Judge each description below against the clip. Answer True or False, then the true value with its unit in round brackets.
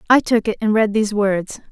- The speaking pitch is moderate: False (215 Hz)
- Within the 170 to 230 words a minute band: False (245 wpm)